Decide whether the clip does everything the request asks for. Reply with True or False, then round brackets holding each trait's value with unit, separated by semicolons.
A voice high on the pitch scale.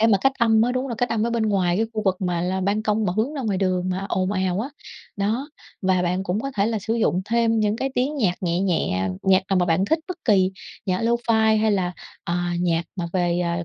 True (200 Hz)